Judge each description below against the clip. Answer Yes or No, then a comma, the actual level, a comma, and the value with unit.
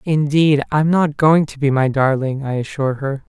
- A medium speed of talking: No, fast, 215 wpm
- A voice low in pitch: No, medium, 145 Hz